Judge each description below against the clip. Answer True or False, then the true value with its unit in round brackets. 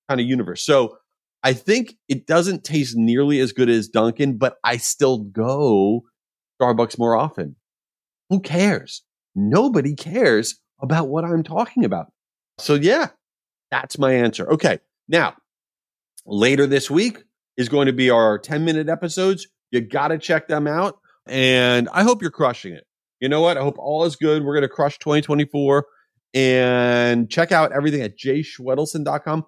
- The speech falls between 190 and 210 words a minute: False (160 wpm)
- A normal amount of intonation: True (4.6 semitones)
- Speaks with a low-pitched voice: False (145 Hz)